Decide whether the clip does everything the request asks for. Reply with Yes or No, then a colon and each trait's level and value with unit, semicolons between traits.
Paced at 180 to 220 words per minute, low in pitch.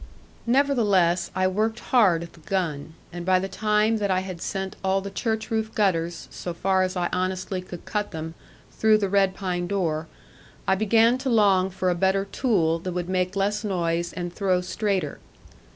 No: average, 185 wpm; high, 190 Hz